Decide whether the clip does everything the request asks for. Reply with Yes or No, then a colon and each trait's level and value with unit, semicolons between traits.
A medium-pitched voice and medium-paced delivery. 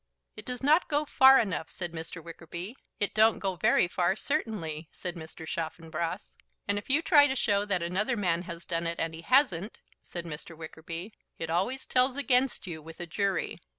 Yes: medium, 180 Hz; average, 190 wpm